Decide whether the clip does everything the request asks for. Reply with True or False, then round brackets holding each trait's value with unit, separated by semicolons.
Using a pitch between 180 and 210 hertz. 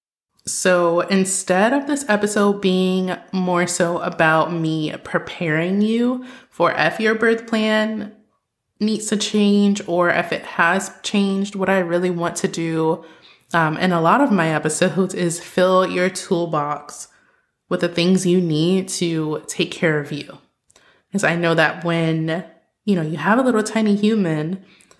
True (185 Hz)